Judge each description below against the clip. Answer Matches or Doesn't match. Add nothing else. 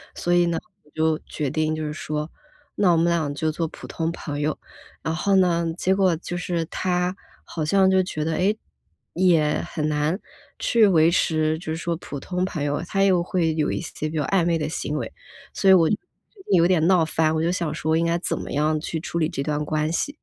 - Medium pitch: Matches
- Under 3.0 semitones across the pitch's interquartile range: Matches